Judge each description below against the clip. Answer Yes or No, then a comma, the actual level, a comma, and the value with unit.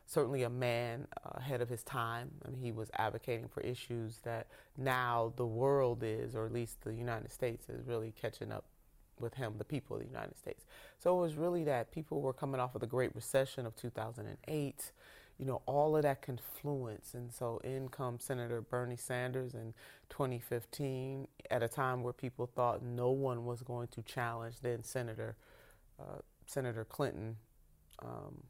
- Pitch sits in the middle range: No, low, 125 Hz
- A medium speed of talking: Yes, average, 180 wpm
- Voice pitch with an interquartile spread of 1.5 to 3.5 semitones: Yes, narrow, 2.4 semitones